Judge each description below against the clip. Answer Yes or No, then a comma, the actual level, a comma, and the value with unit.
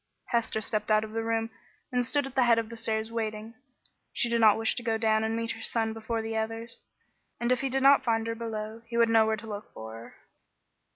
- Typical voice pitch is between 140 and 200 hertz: No, high, 225 Hz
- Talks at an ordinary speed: No, fast, 245 wpm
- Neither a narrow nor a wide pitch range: No, narrow, 1.1 semitones